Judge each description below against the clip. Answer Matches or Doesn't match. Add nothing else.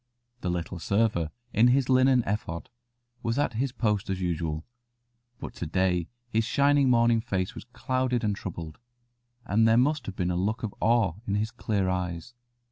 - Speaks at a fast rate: Doesn't match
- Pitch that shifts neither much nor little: Matches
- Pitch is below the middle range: Matches